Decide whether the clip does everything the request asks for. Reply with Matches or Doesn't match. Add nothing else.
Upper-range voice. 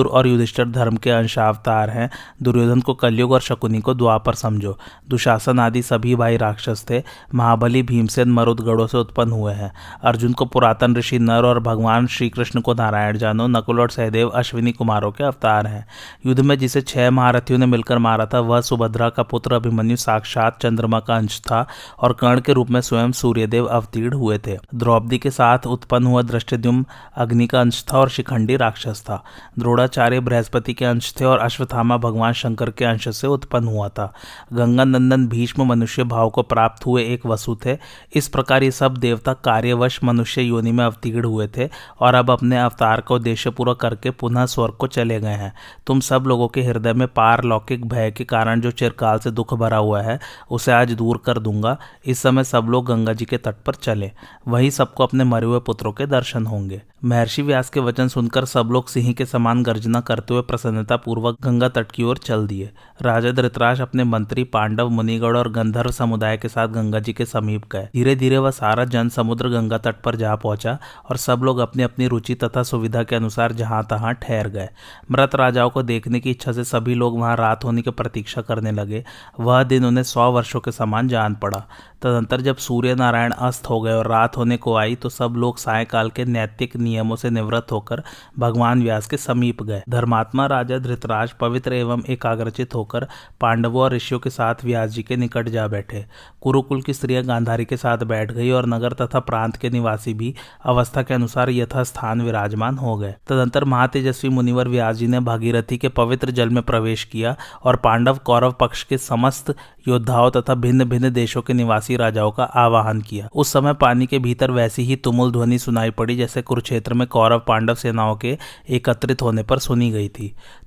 Doesn't match